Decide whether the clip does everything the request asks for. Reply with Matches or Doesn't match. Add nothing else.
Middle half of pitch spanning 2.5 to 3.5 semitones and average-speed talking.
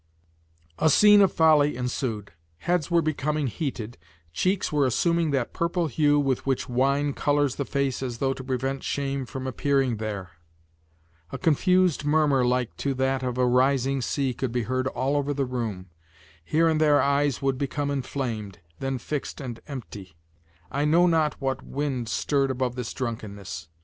Matches